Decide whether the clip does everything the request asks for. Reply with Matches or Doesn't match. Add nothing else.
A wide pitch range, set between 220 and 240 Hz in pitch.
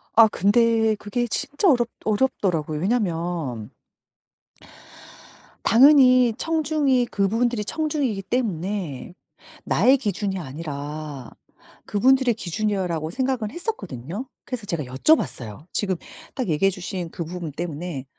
Doesn't match